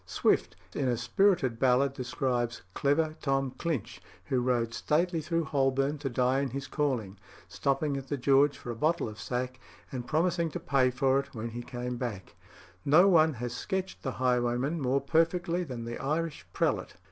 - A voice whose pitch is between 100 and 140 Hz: Yes, low, 135 Hz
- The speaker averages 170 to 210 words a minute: Yes, average, 175 wpm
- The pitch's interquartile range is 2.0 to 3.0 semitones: No, average, 3.9 semitones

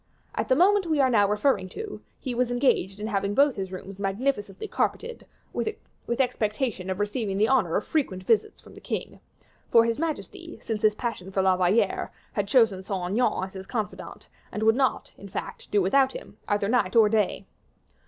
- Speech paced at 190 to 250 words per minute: Yes, average, 195 wpm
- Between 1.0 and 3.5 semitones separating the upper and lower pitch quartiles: No, average, 5.0 semitones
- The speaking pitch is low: No, high, 215 Hz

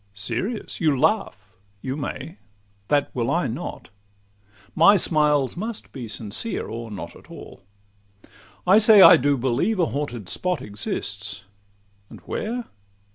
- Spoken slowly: Yes, slow, 125 wpm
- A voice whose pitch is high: No, low, 135 Hz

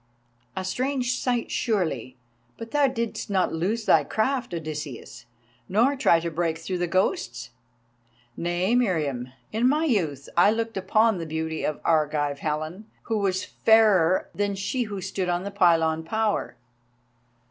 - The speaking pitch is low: No, medium, 185 Hz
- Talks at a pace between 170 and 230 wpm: No, average, 145 wpm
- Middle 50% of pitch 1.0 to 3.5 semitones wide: No, wide, 5.6 semitones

